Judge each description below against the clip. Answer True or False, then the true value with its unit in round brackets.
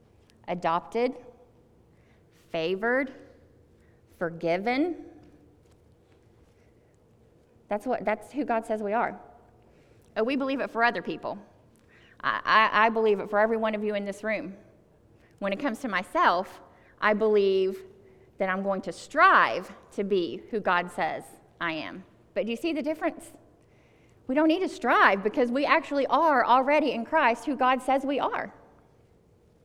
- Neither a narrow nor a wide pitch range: False (7.1 semitones)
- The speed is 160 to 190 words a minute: False (150 wpm)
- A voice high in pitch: True (220 Hz)